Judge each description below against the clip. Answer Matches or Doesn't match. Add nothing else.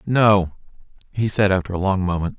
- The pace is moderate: Matches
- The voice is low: Matches